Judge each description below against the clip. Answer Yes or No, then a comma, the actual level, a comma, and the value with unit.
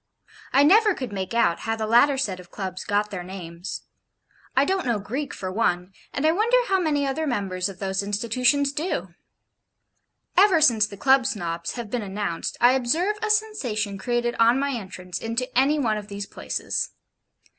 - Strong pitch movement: Yes, wide, 6.1 semitones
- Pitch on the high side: Yes, high, 235 Hz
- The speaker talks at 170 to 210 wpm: Yes, average, 180 wpm